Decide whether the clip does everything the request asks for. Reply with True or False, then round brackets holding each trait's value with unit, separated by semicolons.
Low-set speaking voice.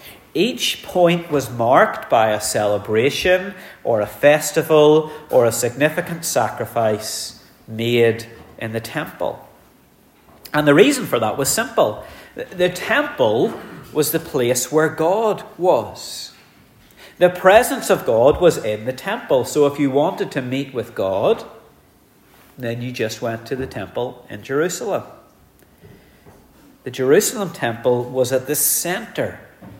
False (145 Hz)